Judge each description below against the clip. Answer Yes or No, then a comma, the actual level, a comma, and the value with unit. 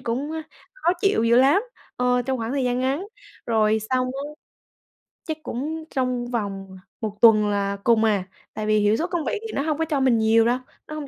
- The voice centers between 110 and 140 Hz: No, very high, 250 Hz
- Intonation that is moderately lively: Yes, average, 4.4 semitones